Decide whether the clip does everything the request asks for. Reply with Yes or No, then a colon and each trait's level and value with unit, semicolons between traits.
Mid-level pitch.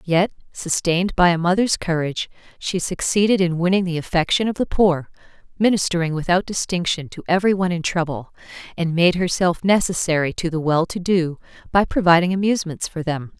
Yes: medium, 175 Hz